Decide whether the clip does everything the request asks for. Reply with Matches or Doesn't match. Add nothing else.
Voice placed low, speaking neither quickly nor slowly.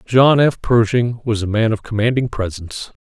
Matches